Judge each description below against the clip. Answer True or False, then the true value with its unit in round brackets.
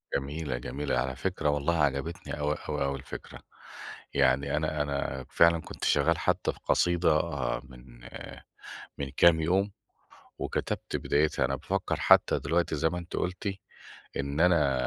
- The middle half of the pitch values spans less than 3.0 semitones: False (3.4 semitones)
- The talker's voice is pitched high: False (75 Hz)